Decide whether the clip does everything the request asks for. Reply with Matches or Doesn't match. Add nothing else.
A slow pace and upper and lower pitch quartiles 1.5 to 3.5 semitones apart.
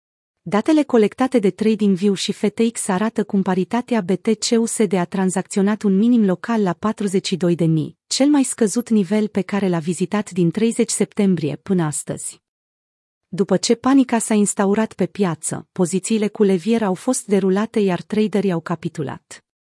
Doesn't match